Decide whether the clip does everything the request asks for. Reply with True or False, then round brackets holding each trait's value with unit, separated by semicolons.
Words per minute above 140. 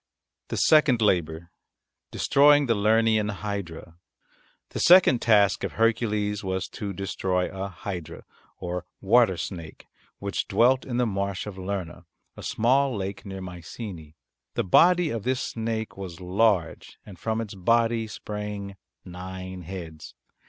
False (135 wpm)